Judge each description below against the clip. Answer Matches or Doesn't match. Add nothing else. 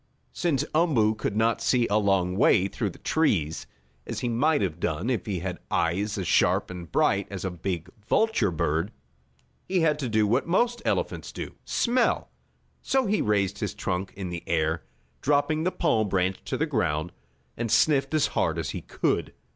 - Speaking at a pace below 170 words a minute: Doesn't match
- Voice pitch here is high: Doesn't match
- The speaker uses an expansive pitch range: Matches